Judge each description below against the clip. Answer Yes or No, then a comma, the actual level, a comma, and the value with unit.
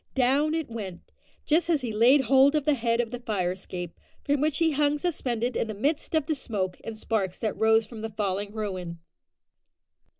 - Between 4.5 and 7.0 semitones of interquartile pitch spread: Yes, wide, 5.4 semitones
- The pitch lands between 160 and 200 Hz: No, high, 235 Hz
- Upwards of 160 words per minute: Yes, average, 200 wpm